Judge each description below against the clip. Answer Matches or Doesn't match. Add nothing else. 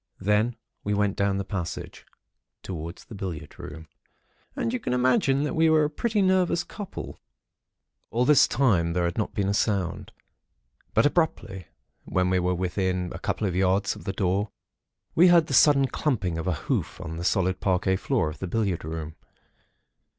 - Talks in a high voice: Doesn't match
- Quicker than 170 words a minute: Matches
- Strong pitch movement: Matches